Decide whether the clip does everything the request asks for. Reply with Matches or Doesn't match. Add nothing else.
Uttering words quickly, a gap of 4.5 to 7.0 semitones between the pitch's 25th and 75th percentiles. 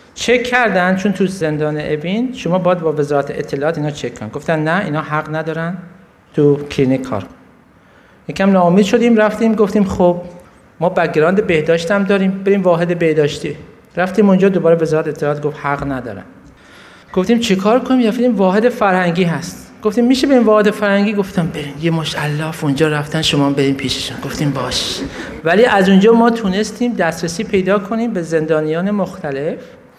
Matches